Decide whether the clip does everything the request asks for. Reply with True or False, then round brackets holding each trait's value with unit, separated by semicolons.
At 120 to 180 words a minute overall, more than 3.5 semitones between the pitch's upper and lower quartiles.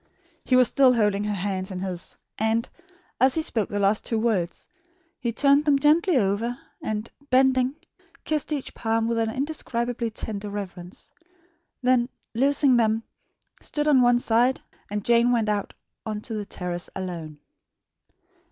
True (150 wpm; 3.9 semitones)